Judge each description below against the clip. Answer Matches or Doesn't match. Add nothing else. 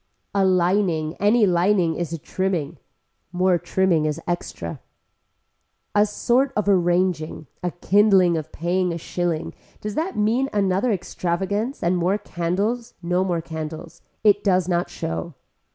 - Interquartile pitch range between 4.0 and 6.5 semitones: Doesn't match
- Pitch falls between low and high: Matches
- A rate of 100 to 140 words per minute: Matches